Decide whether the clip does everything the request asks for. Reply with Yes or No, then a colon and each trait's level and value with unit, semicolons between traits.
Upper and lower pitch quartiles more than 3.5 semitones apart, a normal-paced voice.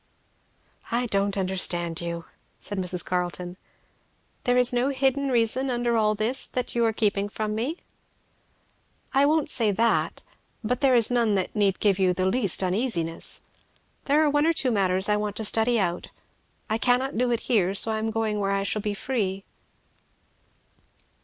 Yes: average, 4.2 semitones; average, 170 wpm